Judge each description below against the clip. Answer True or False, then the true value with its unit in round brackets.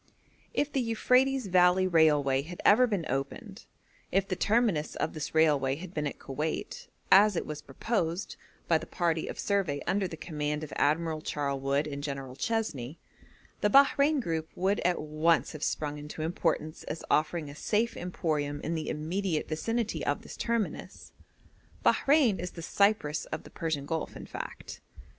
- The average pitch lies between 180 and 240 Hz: False (165 Hz)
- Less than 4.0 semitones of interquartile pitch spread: False (5.1 semitones)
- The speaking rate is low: False (165 wpm)